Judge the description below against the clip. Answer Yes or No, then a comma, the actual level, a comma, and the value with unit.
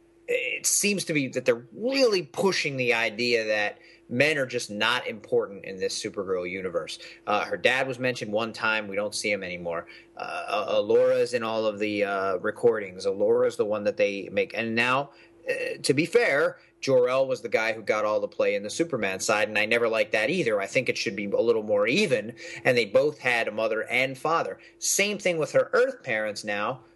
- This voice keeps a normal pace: No, fast, 210 wpm